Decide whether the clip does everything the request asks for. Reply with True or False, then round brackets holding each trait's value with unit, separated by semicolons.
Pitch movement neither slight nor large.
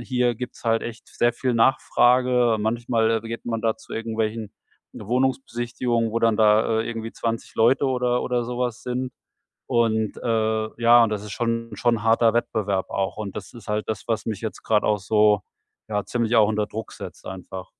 False (1.7 semitones)